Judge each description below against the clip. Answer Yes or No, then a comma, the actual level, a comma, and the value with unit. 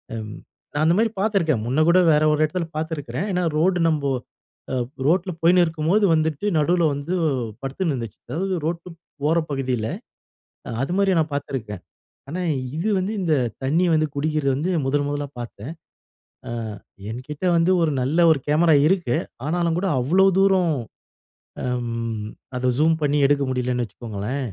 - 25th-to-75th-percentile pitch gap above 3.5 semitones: Yes, average, 4.5 semitones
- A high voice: No, medium, 155 Hz